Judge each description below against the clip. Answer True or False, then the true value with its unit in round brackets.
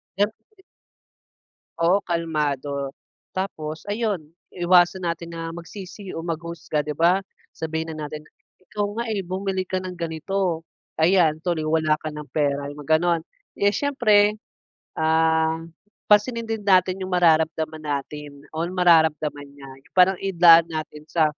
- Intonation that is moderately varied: True (3.1 semitones)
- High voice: False (165 Hz)